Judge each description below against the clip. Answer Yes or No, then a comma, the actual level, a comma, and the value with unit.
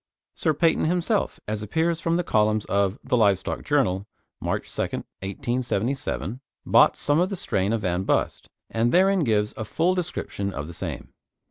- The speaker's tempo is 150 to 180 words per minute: Yes, average, 170 wpm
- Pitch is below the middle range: Yes, low, 120 Hz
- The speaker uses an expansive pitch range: Yes, wide, 8.4 semitones